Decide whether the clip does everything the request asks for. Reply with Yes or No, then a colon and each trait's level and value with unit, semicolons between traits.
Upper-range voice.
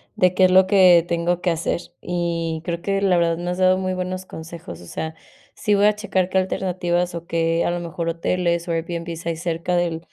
No: medium, 175 Hz